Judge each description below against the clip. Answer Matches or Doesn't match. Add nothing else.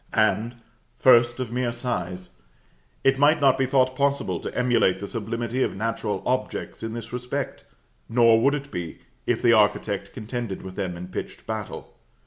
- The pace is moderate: Matches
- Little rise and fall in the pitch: Doesn't match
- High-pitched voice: Doesn't match